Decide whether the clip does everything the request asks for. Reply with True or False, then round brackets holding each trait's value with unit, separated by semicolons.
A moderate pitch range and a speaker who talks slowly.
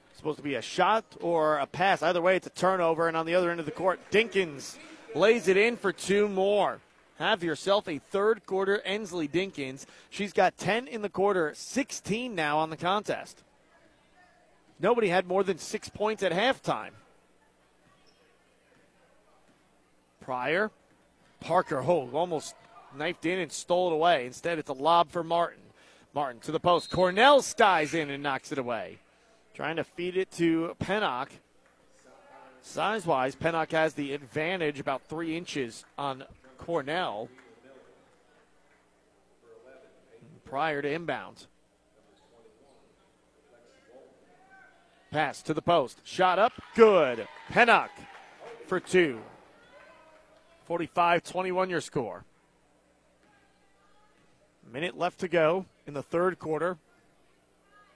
True (3.9 semitones; 130 wpm)